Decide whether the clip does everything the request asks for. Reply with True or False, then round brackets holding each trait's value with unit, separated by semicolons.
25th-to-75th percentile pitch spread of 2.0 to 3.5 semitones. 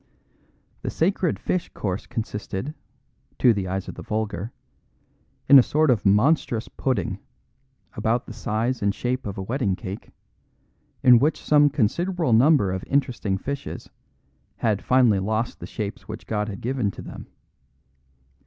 False (4.8 semitones)